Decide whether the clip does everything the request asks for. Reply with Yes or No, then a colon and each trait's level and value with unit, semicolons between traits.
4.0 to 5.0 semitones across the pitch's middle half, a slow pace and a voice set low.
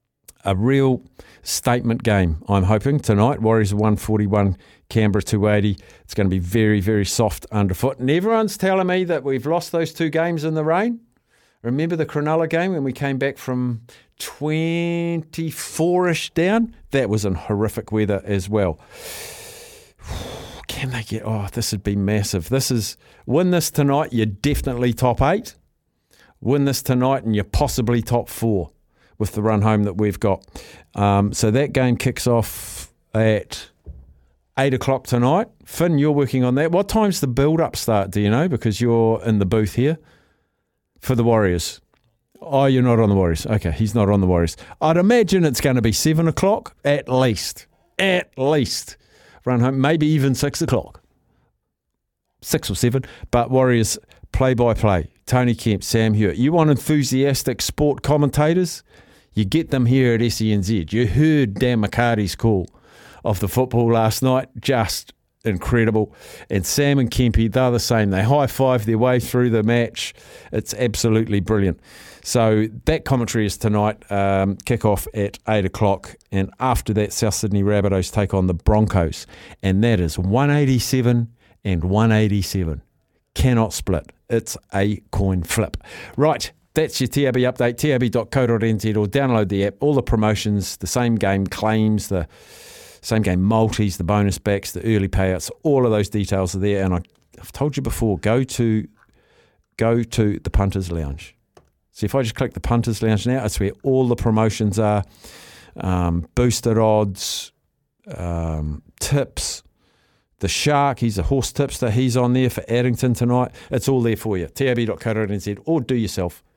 No: average, 4.6 semitones; average, 165 wpm; low, 115 Hz